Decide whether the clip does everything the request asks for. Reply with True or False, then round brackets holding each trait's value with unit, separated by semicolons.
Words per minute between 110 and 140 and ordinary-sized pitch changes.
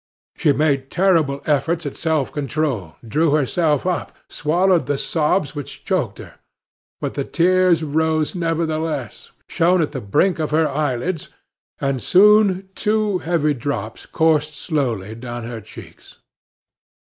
True (135 wpm; 3.7 semitones)